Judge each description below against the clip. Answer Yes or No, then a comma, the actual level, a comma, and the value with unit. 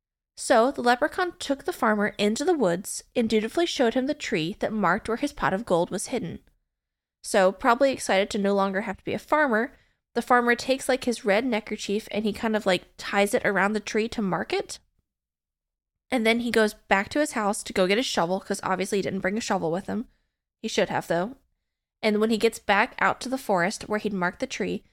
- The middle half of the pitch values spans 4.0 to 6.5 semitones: Yes, average, 4.3 semitones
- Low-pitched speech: No, high, 215 Hz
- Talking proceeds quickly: Yes, fast, 230 wpm